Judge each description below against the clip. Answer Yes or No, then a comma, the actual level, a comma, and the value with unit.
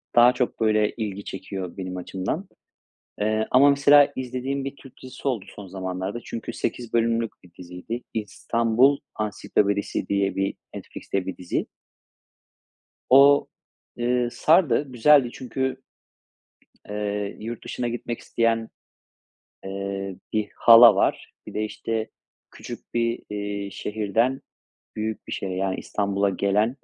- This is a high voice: No, low, 110 Hz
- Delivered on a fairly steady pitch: No, average, 3.8 semitones